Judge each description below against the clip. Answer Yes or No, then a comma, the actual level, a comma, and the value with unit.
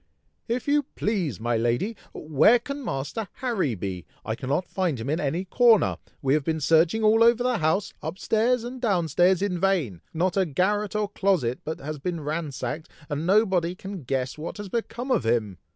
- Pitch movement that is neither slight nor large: No, wide, 6.9 semitones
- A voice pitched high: No, medium, 175 Hz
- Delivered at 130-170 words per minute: No, average, 195 wpm